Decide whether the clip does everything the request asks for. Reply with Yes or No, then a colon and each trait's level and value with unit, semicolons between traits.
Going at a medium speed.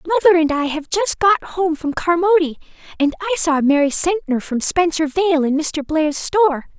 Yes: average, 185 wpm